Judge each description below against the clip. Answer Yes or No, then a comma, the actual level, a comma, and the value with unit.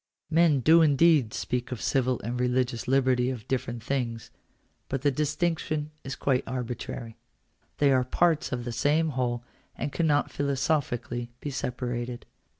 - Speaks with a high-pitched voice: No, low, 130 Hz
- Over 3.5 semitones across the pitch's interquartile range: No, average, 3.1 semitones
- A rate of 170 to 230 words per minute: No, average, 145 wpm